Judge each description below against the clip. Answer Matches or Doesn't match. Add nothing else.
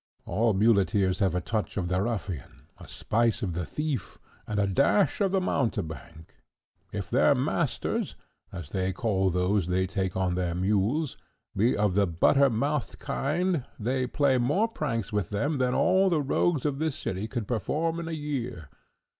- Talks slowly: Doesn't match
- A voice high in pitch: Doesn't match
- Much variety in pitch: Matches